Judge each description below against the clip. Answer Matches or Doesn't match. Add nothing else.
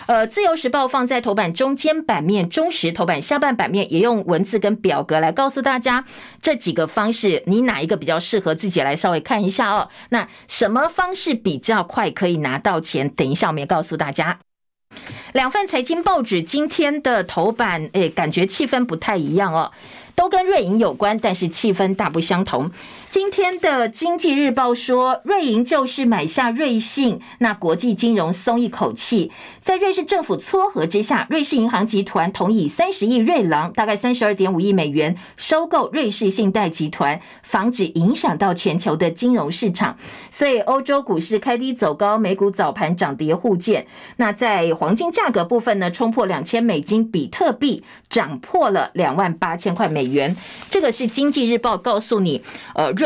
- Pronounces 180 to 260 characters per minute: Doesn't match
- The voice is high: Matches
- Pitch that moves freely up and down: Matches